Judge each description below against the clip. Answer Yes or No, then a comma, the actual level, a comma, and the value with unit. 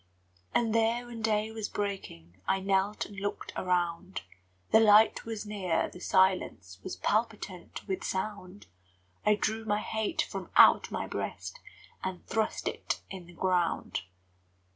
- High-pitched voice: Yes, high, 200 Hz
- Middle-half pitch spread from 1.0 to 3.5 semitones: Yes, average, 3.0 semitones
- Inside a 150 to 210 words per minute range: No, average, 140 wpm